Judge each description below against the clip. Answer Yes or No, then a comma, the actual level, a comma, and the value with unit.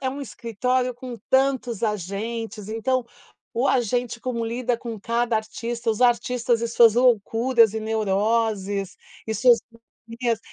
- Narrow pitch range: Yes, narrow, 2.0 semitones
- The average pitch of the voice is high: Yes, high, 235 Hz